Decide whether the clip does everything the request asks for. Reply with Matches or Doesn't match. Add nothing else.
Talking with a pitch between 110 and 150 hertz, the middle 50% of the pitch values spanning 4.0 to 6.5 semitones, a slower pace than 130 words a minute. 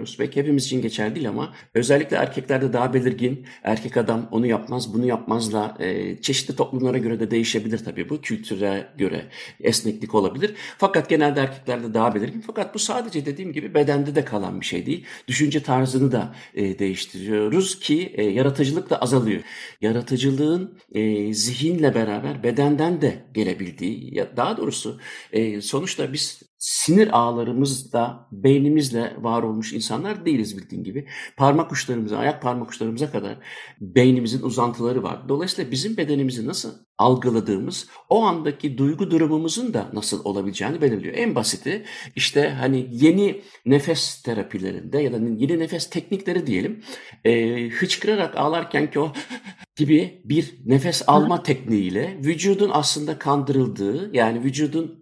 Doesn't match